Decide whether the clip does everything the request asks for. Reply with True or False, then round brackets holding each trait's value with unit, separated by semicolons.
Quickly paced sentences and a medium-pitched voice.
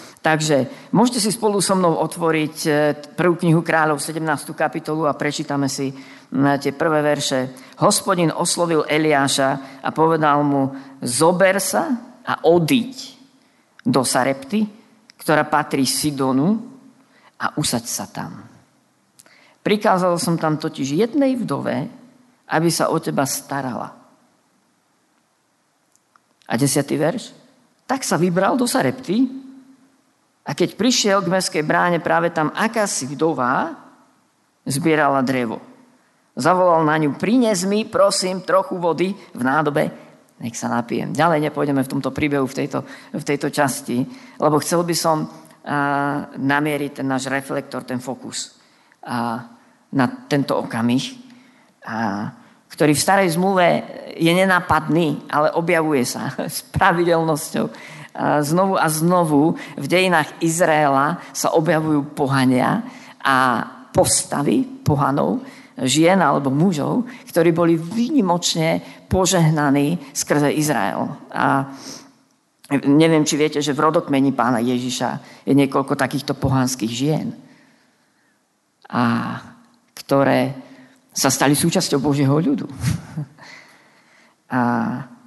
False (115 wpm; 155 Hz)